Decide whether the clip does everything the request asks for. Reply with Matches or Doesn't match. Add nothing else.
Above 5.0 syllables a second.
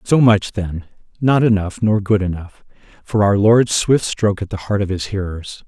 Doesn't match